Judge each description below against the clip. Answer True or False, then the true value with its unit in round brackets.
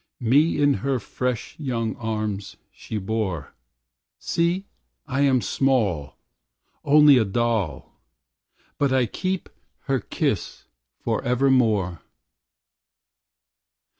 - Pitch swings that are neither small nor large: True (4.4 semitones)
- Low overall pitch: True (120 Hz)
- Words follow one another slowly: True (90 wpm)